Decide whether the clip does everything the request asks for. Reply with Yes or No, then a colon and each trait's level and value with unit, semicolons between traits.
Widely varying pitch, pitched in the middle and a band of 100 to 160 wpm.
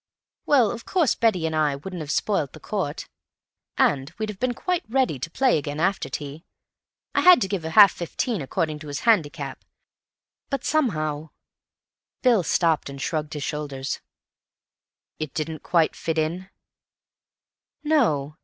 Yes: wide, 6.5 semitones; medium, 165 Hz; average, 145 wpm